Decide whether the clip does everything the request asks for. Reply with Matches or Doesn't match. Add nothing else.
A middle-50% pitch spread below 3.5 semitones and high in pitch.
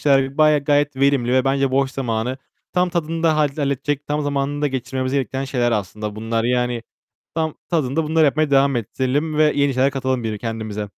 Doesn't match